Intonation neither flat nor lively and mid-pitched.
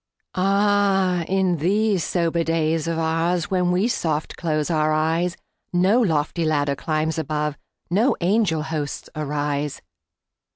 Yes: average, 3.2 semitones; medium, 165 Hz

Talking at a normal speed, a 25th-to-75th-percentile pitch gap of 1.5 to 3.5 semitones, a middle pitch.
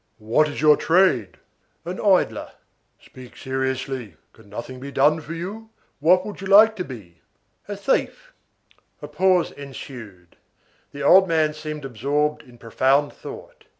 No: average, 145 wpm; wide, 5.5 semitones; medium, 145 Hz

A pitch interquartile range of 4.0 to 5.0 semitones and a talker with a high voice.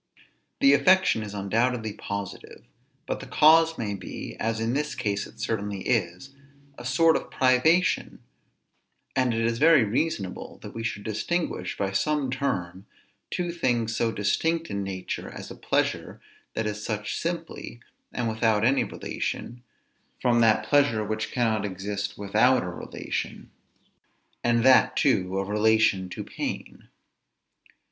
No: average, 4.7 semitones; low, 115 Hz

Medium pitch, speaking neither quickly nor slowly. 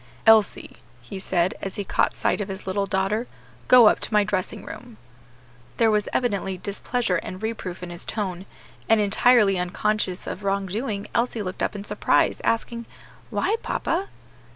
No: high, 205 Hz; average, 160 wpm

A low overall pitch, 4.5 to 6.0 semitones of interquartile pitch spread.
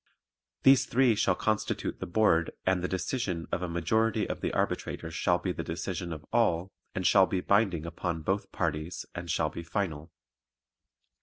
No: very low, 90 Hz; average, 3.3 semitones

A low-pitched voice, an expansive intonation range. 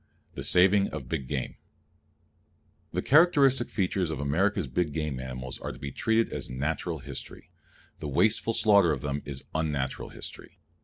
Yes: very low, 80 Hz; wide, 6.6 semitones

